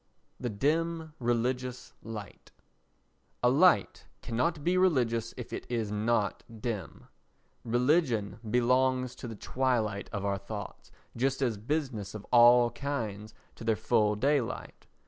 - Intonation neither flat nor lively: Yes, average, 3.5 semitones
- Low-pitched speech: Yes, low, 120 Hz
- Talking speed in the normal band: No, slow, 125 wpm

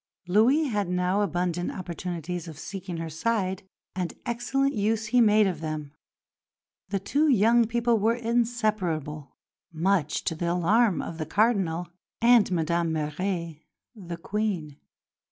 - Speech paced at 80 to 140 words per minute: Yes, slow, 135 wpm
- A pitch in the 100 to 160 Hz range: No, medium, 185 Hz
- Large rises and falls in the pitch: No, average, 5.0 semitones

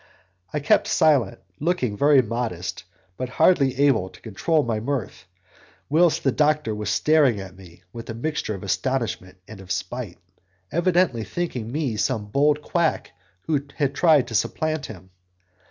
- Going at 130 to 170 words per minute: Yes, average, 155 wpm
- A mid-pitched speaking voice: No, low, 125 Hz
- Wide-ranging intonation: Yes, wide, 6.1 semitones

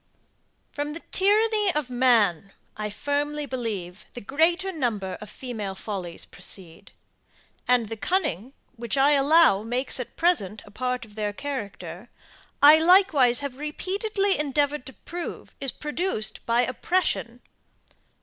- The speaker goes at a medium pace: No, slow, 130 wpm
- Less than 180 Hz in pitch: No, very high, 255 Hz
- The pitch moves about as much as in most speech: No, wide, 6.1 semitones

